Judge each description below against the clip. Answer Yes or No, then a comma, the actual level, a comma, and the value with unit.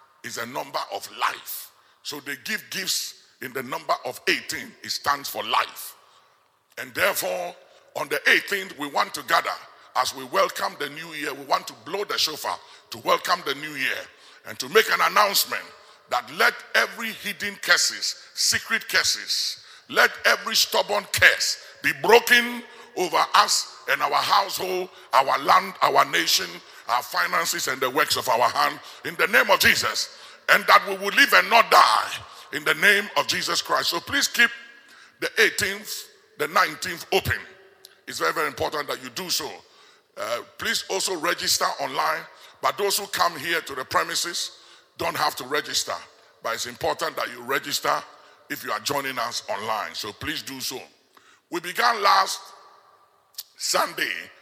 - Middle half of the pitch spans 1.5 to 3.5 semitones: No, average, 4.4 semitones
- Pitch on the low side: No, high, 205 Hz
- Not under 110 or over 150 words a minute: No, average, 165 wpm